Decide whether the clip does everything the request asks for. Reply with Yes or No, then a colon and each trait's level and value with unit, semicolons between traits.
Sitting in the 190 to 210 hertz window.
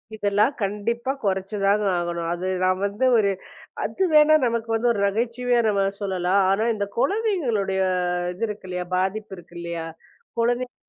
Yes: high, 205 Hz